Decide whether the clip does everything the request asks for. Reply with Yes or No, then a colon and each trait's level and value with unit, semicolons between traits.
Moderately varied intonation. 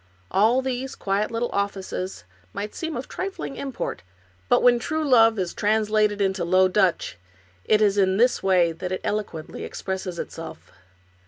Yes: average, 4.2 semitones